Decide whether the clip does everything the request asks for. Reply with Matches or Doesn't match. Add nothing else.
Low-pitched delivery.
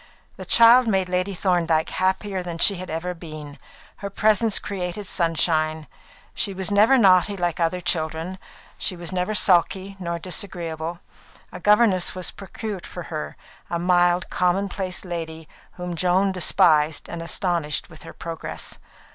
Doesn't match